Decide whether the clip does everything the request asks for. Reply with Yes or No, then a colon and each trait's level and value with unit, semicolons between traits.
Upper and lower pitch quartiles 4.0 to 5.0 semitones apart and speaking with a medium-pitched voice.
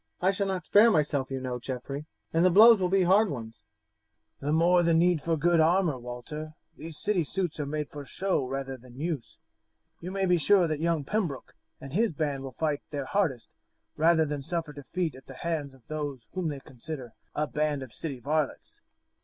Yes: average, 4.3 semitones; medium, 155 Hz